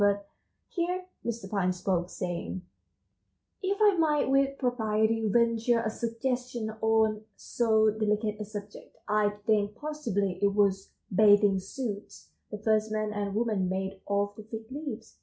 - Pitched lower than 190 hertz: No, high, 215 Hz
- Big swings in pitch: No, average, 2.7 semitones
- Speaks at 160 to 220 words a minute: No, average, 140 wpm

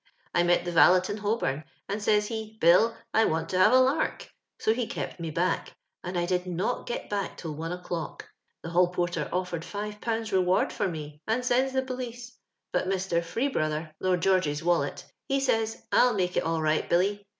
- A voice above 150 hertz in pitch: Yes, medium, 185 Hz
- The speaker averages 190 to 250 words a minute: Yes, average, 200 wpm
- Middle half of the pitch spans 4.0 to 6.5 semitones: Yes, average, 4.6 semitones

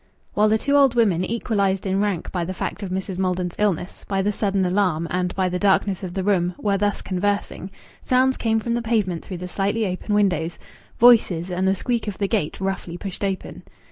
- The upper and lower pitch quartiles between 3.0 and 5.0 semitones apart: No, narrow, 2.4 semitones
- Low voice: No, high, 195 Hz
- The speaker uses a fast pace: Yes, fast, 210 wpm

